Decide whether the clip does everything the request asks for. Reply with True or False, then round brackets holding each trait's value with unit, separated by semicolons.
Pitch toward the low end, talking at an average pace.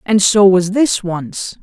False (200 Hz; 185 wpm)